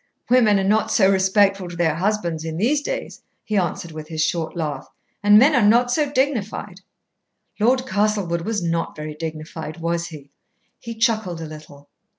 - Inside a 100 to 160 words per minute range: No, average, 170 wpm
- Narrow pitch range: No, average, 5.2 semitones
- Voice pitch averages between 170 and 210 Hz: Yes, high, 190 Hz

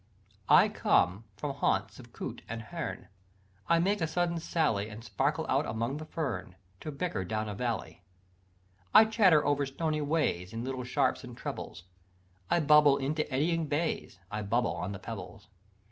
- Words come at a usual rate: Yes, average, 165 wpm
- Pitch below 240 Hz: Yes, medium, 140 Hz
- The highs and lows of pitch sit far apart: Yes, wide, 6.4 semitones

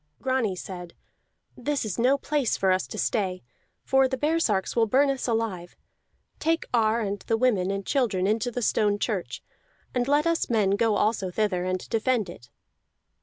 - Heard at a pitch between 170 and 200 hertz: No, high, 220 Hz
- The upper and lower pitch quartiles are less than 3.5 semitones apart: No, average, 4.9 semitones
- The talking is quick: No, average, 170 wpm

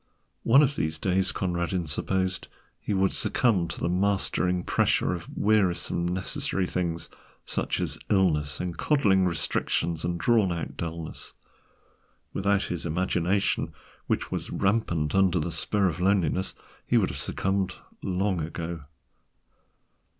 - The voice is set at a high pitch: No, very low, 90 Hz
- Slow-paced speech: Yes, slow, 130 wpm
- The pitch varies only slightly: Yes, narrow, 2.2 semitones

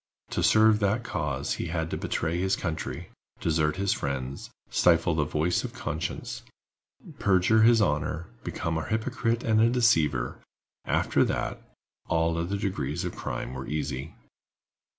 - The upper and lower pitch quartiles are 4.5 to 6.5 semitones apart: Yes, average, 5.1 semitones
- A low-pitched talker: Yes, very low, 85 Hz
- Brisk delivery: No, average, 145 wpm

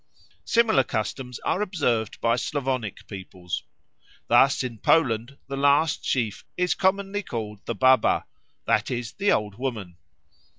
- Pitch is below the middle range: Yes, low, 125 Hz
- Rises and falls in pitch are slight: No, average, 4.5 semitones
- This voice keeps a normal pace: No, slow, 130 wpm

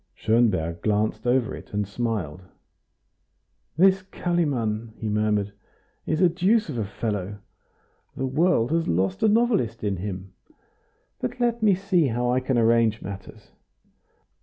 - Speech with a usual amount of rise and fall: No, wide, 8.5 semitones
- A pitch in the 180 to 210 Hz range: No, low, 115 Hz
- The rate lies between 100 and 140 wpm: Yes, slow, 135 wpm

